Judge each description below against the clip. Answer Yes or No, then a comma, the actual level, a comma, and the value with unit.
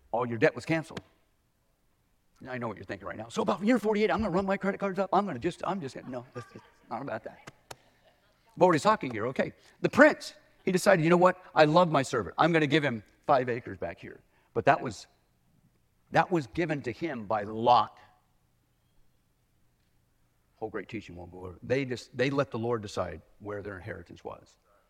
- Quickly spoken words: Yes, fast, 210 wpm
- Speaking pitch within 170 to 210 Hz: No, low, 135 Hz